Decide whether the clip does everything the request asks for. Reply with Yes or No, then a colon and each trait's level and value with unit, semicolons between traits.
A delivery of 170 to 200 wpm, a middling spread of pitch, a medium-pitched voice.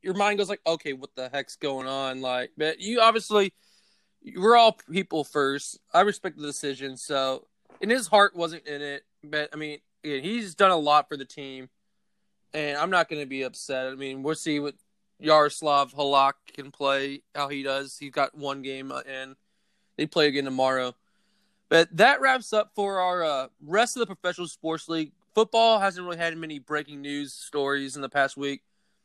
Yes: average, 190 wpm; average, 4.7 semitones; medium, 150 Hz